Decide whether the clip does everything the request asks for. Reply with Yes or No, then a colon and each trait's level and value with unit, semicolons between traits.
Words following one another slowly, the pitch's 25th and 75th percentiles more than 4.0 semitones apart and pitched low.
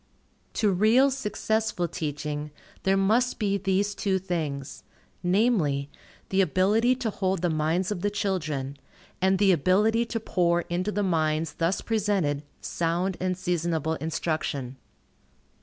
No: slow, 130 wpm; average, 4.4 semitones; medium, 185 Hz